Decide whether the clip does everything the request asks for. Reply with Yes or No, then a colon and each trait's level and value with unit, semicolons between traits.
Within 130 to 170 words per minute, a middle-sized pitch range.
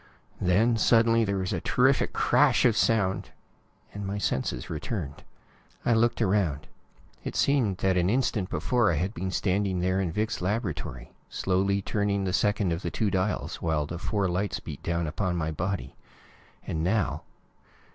Yes: average, 165 wpm; average, 3.3 semitones